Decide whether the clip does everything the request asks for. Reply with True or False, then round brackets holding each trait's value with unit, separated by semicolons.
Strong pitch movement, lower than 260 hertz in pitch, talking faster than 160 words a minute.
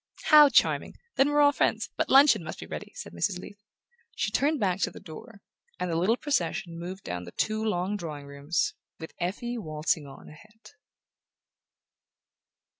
True (6.6 semitones; 190 Hz; 170 wpm)